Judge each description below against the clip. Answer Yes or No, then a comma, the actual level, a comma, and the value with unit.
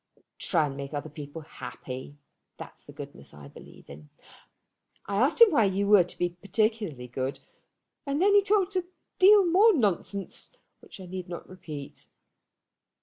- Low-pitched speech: No, medium, 185 Hz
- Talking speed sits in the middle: Yes, average, 160 wpm